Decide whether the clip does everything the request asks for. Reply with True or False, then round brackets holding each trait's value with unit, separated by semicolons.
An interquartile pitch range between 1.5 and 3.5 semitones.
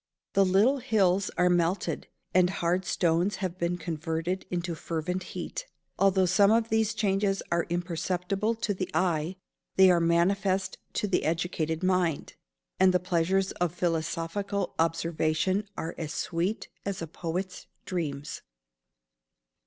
True (2.6 semitones)